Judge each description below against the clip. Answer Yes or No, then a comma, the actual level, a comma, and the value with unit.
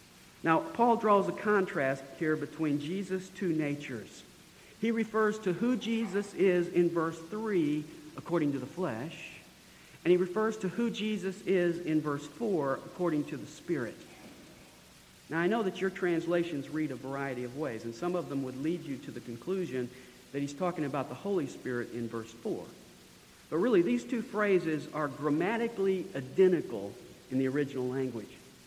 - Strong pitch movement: Yes, wide, 5.7 semitones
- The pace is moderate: Yes, average, 165 wpm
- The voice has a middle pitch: Yes, medium, 165 Hz